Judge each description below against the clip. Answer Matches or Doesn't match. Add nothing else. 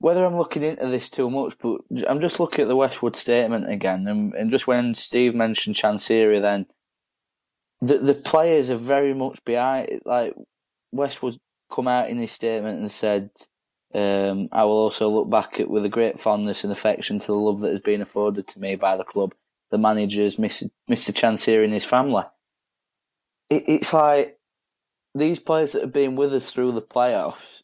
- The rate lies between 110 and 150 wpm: Doesn't match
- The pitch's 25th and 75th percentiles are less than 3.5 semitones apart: Doesn't match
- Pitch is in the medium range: Doesn't match